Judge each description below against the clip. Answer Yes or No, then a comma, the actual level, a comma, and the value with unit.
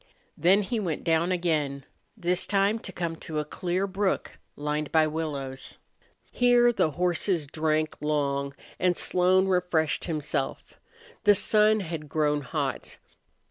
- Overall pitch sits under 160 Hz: No, medium, 165 Hz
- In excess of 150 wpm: No, slow, 135 wpm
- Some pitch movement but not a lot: Yes, average, 3.9 semitones